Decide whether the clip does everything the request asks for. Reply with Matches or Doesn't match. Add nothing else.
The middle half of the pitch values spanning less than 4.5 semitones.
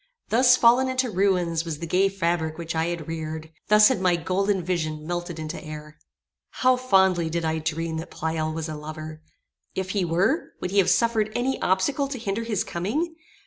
Doesn't match